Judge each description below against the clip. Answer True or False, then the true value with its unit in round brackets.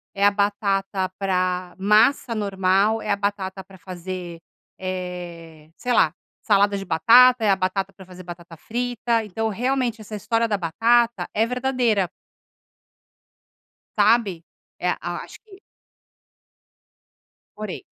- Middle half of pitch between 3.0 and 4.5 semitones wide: True (3.6 semitones)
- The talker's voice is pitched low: False (200 Hz)